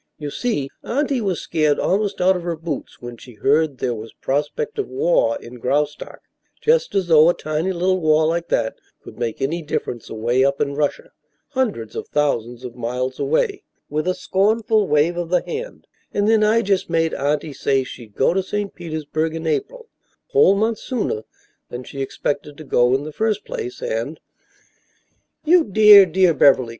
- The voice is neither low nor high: Yes, medium, 165 Hz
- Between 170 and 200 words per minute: Yes, average, 190 wpm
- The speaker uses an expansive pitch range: Yes, wide, 7.2 semitones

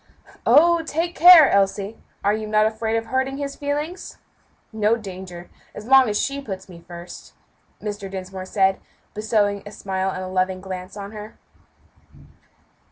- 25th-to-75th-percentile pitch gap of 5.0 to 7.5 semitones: Yes, wide, 5.4 semitones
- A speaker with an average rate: Yes, average, 150 wpm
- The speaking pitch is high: Yes, high, 210 Hz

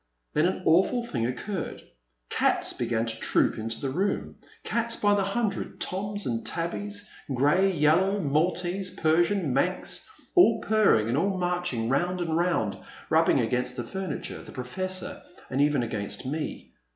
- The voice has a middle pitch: Yes, medium, 175 Hz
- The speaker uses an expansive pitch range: Yes, wide, 6.9 semitones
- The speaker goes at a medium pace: Yes, average, 150 wpm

